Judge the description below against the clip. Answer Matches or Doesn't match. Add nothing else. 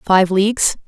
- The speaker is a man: Doesn't match